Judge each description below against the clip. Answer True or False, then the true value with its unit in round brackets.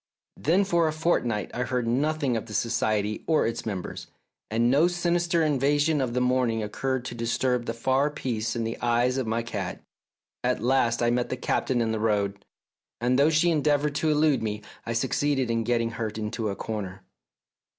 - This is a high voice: False (120 Hz)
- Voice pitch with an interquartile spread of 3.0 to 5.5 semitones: True (4.3 semitones)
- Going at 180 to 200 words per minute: True (190 wpm)